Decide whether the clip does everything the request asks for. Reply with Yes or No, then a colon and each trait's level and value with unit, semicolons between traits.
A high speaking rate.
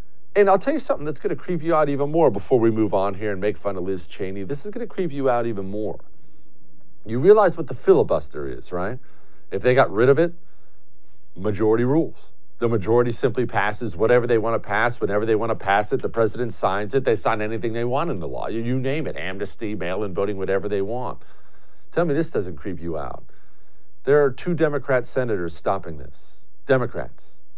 Yes: fast, 210 wpm